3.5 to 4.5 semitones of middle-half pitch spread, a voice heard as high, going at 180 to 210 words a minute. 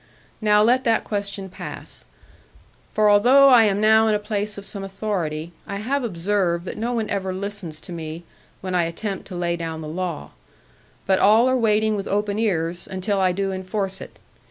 No: average, 3.0 semitones; high, 200 Hz; average, 190 wpm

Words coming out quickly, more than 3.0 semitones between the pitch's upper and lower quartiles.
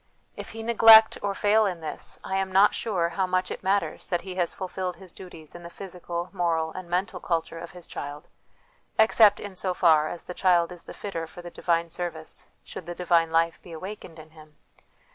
No: fast, 210 wpm; narrow, 2.4 semitones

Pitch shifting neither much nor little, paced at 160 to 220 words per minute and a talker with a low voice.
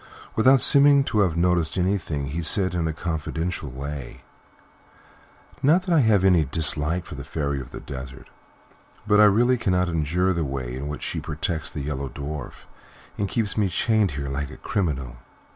No: wide, 5.9 semitones; average, 175 wpm; very low, 85 Hz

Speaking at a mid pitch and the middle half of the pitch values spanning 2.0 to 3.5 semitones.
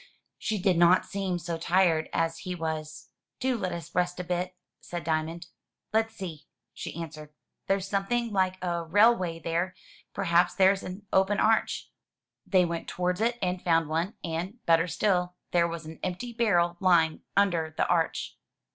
Yes: medium, 180 Hz; average, 2.7 semitones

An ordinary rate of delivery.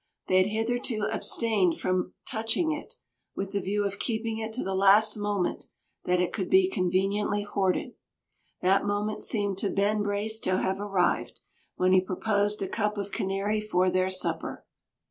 Yes: average, 165 wpm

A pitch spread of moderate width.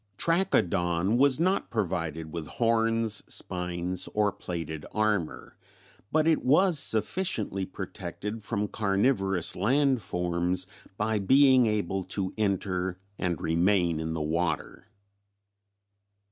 Yes: average, 4.5 semitones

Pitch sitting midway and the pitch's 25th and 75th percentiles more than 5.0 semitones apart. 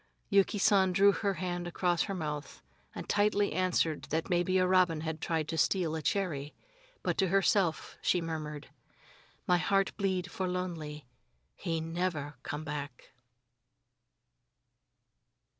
No: medium, 175 Hz; average, 3.2 semitones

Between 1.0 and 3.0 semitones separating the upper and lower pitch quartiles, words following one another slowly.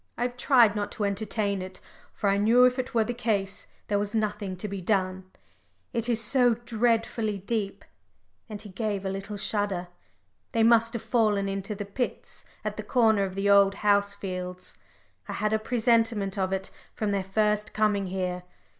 No: narrow, 2.4 semitones; average, 190 wpm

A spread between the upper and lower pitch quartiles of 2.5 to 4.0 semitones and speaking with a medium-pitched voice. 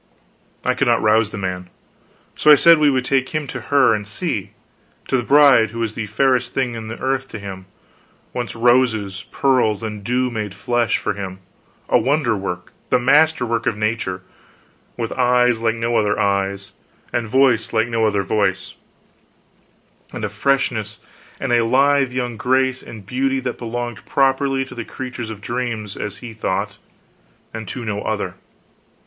No: average, 3.6 semitones; low, 115 Hz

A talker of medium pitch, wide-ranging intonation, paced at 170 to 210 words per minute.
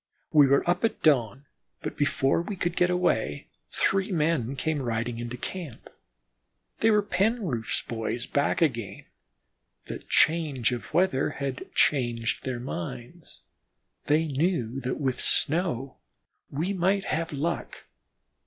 No: medium, 145 Hz; wide, 5.9 semitones; slow, 135 wpm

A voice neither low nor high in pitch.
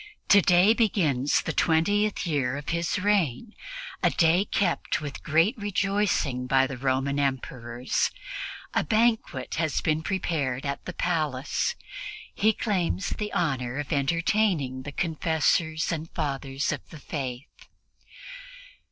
Yes: medium, 155 Hz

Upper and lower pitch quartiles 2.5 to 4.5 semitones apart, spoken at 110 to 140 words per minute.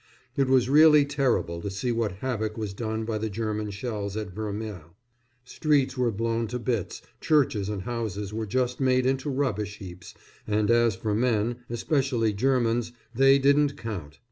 No: average, 3.6 semitones; average, 165 wpm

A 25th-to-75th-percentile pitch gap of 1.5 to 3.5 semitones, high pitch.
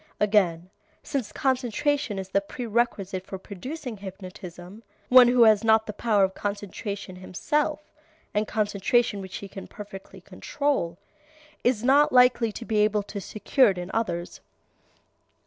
No: average, 3.9 semitones; high, 210 Hz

